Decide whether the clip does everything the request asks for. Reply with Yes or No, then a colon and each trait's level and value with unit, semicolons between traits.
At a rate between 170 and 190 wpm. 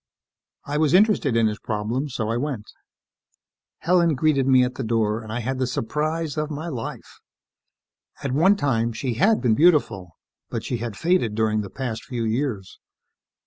Yes: average, 175 wpm